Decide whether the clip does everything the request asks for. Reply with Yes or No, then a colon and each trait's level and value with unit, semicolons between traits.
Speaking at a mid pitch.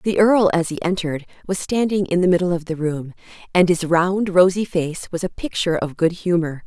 Yes: medium, 175 Hz